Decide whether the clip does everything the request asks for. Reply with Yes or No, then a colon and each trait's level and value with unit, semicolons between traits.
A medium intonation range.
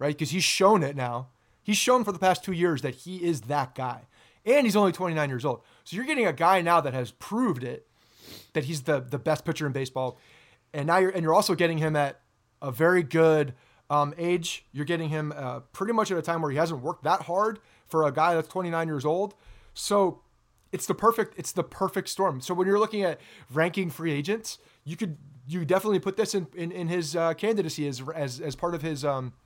Yes: average, 4.5 semitones